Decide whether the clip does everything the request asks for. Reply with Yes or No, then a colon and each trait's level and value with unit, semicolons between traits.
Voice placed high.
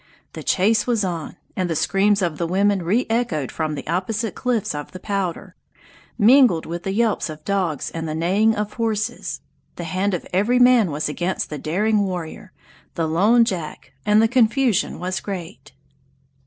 Yes: high, 195 Hz